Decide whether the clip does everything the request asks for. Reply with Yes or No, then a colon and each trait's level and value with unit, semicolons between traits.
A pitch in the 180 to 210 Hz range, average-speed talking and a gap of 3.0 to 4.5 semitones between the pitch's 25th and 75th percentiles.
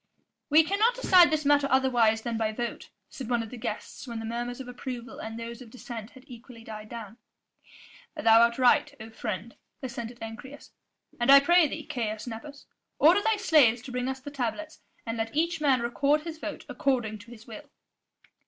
No: high, 245 Hz; average, 190 wpm; average, 4.1 semitones